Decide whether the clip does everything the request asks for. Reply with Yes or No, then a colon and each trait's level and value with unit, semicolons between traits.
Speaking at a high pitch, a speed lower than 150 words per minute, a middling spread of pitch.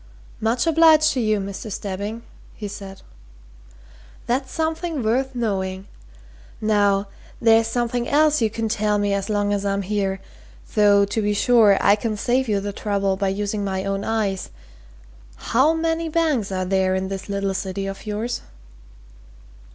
No: high, 210 Hz; average, 155 wpm; average, 3.4 semitones